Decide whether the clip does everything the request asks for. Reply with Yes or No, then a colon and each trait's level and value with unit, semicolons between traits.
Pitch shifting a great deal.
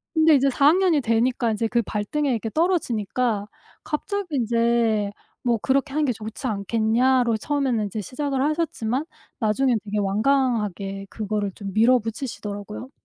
No: average, 4.4 semitones